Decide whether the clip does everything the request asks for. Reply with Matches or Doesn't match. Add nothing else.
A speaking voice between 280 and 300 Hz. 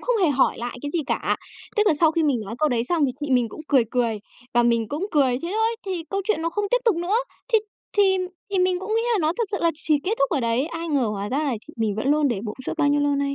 Matches